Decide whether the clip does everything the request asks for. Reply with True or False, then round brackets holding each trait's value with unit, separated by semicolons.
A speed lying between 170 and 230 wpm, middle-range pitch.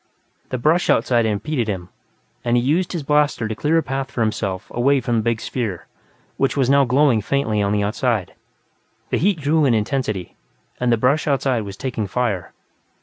False (190 wpm; 120 Hz)